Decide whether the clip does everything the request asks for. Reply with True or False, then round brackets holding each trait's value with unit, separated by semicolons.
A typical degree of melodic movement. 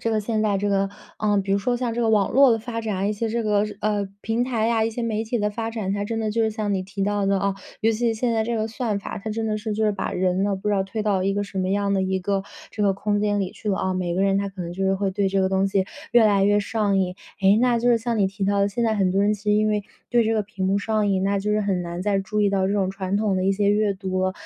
False (2.1 semitones)